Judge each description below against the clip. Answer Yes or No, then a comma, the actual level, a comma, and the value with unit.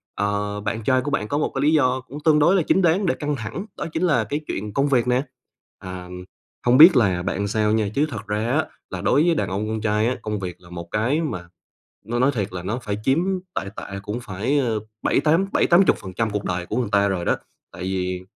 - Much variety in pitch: Yes, wide, 5.9 semitones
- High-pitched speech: No, low, 110 Hz